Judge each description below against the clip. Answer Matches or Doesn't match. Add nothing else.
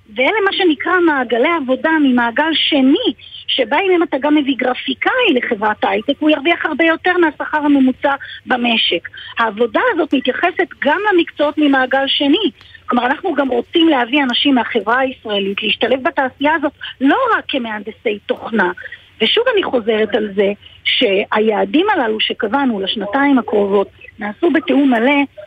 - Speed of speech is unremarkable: Matches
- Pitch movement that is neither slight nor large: Matches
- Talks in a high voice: Matches